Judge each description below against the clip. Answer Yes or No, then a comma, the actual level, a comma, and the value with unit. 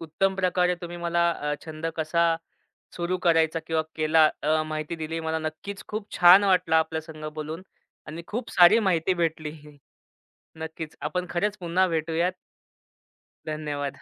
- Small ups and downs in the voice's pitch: Yes, narrow, 2.3 semitones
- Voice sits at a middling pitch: Yes, medium, 165 Hz